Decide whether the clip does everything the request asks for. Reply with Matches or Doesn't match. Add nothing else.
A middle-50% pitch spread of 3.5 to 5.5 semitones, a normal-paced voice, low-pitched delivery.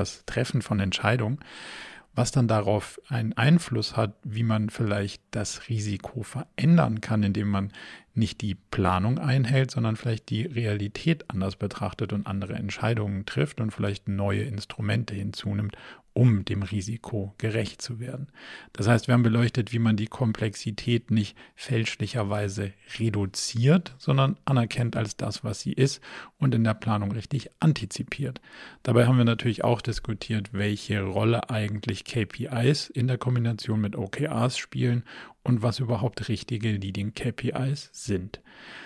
Doesn't match